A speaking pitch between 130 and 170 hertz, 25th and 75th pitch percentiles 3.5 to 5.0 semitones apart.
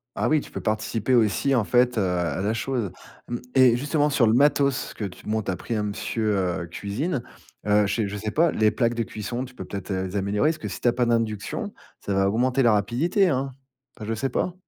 No: low, 115 Hz; average, 4.1 semitones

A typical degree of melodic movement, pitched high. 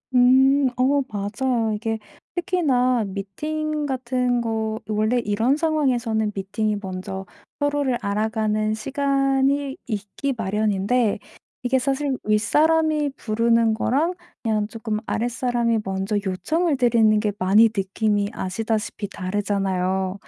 Yes: average, 4.3 semitones; high, 225 Hz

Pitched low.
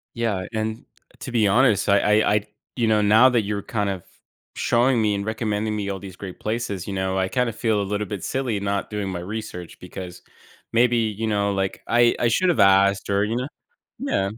Yes: low, 105 Hz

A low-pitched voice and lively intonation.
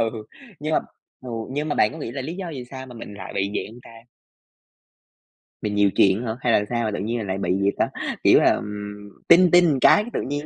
Yes: low, 115 Hz; wide, 5.9 semitones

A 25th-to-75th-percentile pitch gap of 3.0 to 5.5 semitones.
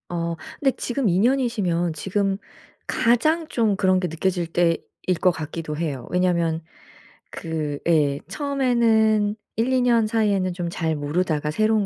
Yes: average, 5.2 semitones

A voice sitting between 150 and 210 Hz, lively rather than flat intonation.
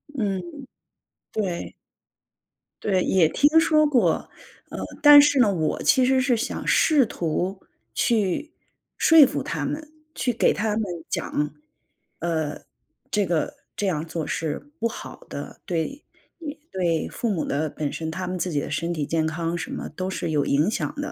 Yes: medium, 185 Hz; wide, 7.6 semitones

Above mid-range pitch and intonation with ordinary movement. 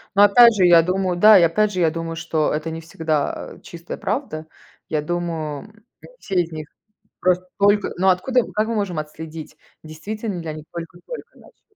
No: medium, 175 Hz; average, 3.9 semitones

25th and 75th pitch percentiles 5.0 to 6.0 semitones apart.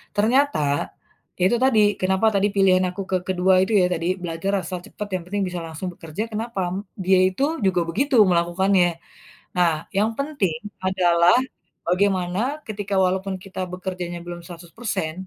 No: narrow, 2.4 semitones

